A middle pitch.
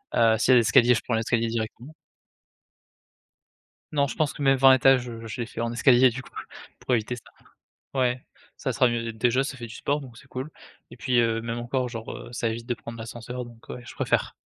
No: low, 120 Hz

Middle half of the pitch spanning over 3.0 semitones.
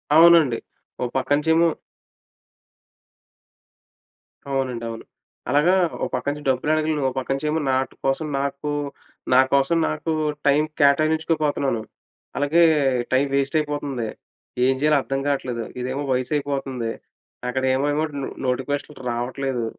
No: narrow, 2.6 semitones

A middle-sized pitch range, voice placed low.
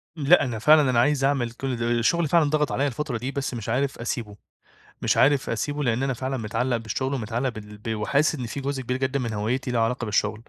Yes: average, 3.4 semitones; low, 125 Hz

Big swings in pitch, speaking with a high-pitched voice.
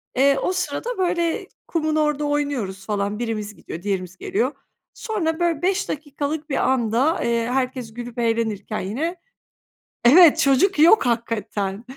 Yes: wide, 6.4 semitones; very high, 270 Hz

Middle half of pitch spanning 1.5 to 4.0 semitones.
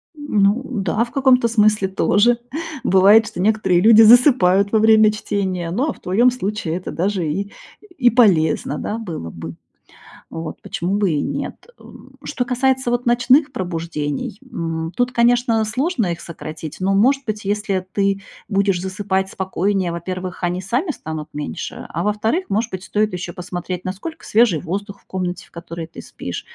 No: average, 4.4 semitones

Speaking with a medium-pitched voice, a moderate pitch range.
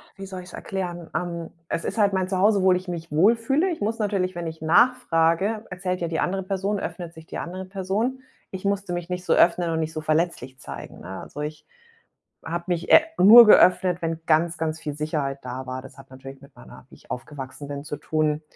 Yes: medium, 175 Hz; average, 3.6 semitones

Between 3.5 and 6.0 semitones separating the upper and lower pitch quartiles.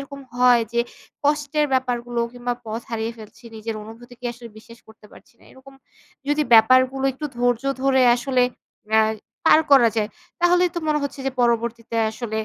No: average, 2.8 semitones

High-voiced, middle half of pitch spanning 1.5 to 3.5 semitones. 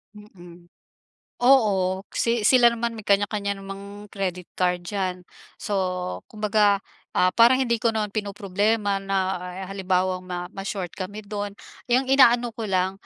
Yes: high, 200 Hz; average, 2.8 semitones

